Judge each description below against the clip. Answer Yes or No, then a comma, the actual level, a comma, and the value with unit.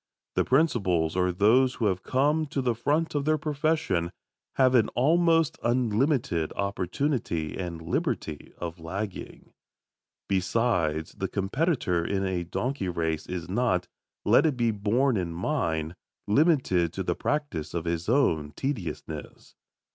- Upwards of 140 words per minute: No, slow, 135 wpm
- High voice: No, low, 105 Hz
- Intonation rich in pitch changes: Yes, wide, 7.9 semitones